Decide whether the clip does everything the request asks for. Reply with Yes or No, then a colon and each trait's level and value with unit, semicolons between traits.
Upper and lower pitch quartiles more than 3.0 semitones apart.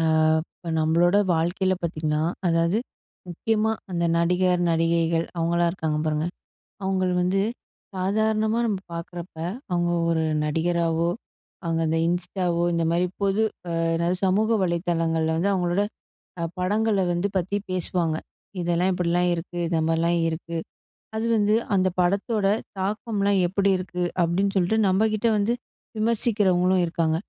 No: average, 2.7 semitones